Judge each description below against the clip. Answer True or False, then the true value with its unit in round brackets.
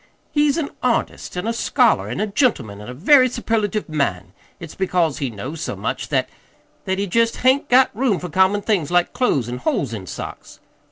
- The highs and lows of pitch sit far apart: True (9.0 semitones)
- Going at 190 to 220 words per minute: True (200 wpm)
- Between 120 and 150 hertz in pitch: False (190 Hz)